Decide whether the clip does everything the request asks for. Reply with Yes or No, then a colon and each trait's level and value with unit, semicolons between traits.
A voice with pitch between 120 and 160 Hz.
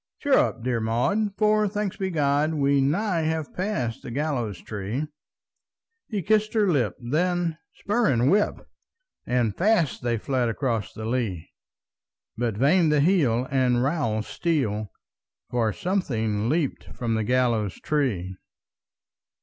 Yes: low, 135 Hz